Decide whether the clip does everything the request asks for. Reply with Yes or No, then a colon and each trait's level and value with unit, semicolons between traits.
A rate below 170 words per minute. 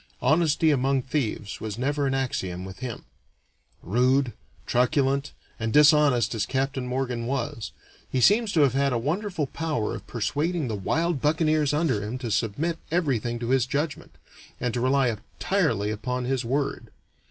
Yes: average, 155 wpm